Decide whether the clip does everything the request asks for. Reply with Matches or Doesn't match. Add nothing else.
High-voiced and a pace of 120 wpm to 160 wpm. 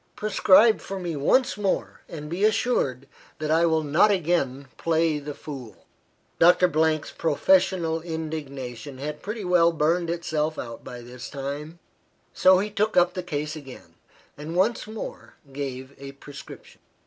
Doesn't match